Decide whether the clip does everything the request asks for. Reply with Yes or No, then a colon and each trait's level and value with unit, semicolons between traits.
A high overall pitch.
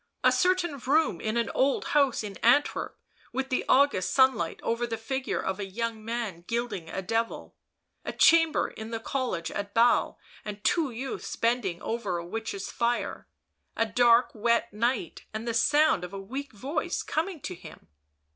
Yes: high, 235 Hz